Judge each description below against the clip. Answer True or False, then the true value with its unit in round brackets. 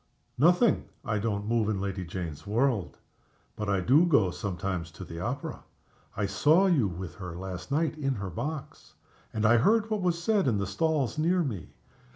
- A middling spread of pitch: False (8.4 semitones)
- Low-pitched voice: True (110 Hz)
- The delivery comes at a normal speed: True (185 wpm)